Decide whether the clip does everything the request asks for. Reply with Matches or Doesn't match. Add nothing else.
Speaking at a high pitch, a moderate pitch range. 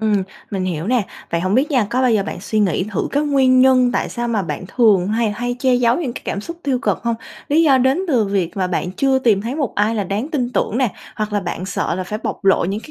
Matches